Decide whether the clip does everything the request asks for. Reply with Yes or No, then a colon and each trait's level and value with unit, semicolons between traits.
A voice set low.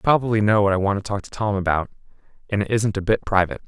Yes: low, 100 Hz